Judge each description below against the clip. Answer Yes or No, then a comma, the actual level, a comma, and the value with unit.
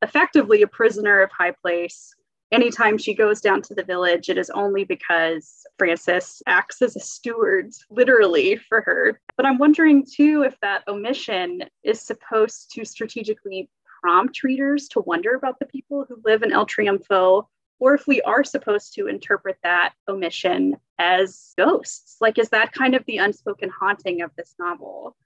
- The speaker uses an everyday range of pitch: No, wide, 6.3 semitones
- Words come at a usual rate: Yes, average, 165 wpm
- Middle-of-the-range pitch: No, high, 220 Hz